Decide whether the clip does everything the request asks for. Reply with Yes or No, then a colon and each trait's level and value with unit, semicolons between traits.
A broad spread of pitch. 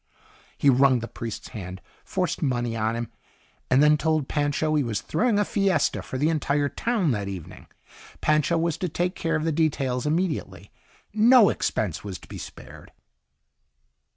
Yes: wide, 5.8 semitones